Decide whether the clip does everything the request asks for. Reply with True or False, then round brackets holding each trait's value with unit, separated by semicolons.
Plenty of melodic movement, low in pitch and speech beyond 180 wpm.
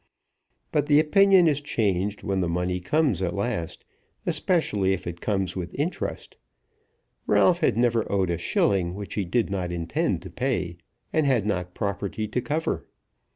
False (7.3 semitones; 100 Hz; 160 wpm)